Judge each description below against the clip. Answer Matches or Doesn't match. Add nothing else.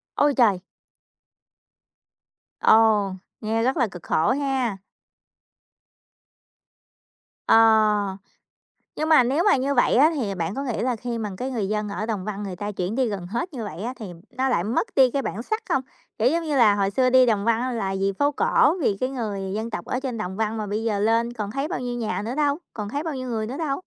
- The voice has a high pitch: Matches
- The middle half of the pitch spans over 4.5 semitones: Doesn't match